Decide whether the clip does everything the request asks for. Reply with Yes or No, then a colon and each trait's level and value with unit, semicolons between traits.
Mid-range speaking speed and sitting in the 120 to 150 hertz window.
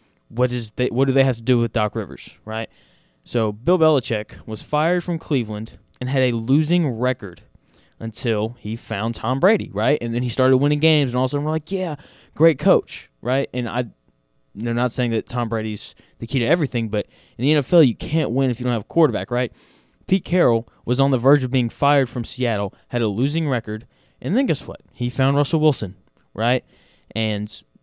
No: fast, 215 wpm; low, 125 Hz